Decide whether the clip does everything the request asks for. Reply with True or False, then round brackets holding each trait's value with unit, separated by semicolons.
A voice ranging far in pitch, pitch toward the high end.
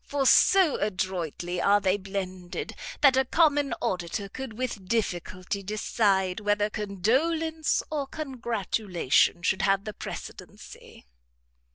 True (5.9 semitones; 205 Hz)